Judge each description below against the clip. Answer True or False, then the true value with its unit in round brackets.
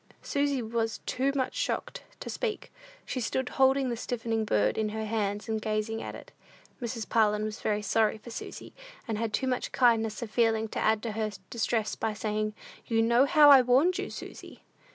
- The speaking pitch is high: True (225 Hz)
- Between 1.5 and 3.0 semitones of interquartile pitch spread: True (2.7 semitones)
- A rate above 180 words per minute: True (195 wpm)